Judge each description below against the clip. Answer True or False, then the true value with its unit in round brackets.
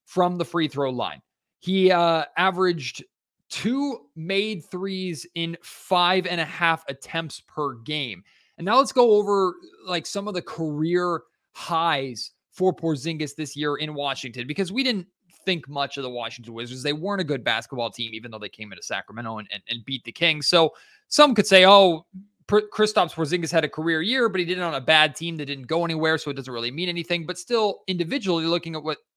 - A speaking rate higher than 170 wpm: True (200 wpm)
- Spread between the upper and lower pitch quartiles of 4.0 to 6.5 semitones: True (4.5 semitones)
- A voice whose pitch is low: False (165 Hz)